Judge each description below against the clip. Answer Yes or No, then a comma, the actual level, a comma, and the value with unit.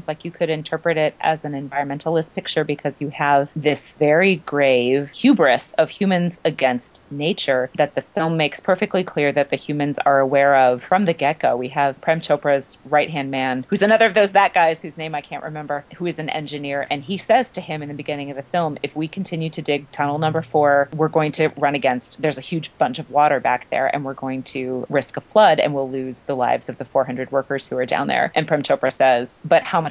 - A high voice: No, medium, 150 Hz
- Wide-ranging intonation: No, average, 2.7 semitones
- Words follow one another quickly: Yes, fast, 235 wpm